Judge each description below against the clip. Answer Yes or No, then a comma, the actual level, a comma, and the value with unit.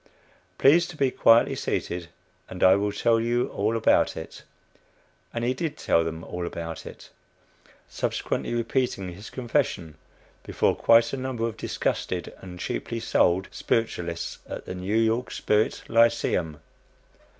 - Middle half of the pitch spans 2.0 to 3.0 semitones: No, average, 5.0 semitones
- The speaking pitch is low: Yes, low, 110 Hz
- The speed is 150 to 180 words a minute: No, average, 140 wpm